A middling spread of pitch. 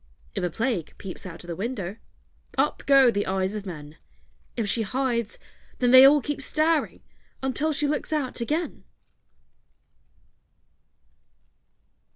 No: wide, 6.3 semitones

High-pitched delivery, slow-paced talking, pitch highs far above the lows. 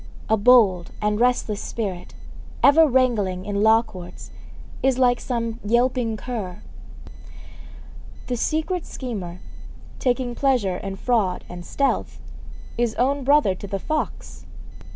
No: high, 230 Hz; slow, 120 wpm; average, 4.2 semitones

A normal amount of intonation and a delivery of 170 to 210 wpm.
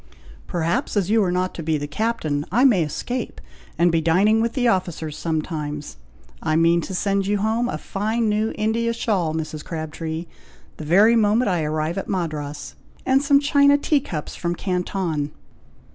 No: wide, 5.7 semitones; average, 175 wpm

